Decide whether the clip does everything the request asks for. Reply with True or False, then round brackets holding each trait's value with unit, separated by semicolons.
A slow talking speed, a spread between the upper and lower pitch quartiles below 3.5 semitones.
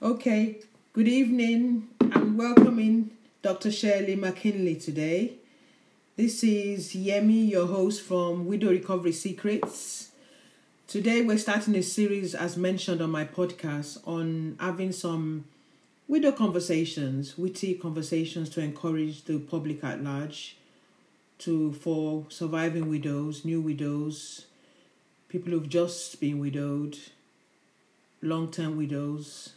False (110 wpm; 5.2 semitones)